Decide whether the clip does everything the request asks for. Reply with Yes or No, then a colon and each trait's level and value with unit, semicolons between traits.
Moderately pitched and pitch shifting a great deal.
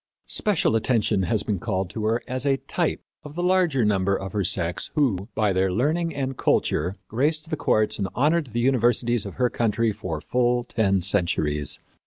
No: low, 115 Hz; wide, 5.7 semitones